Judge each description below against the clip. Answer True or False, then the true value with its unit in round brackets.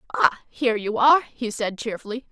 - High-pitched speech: True (235 Hz)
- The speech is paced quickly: False (180 wpm)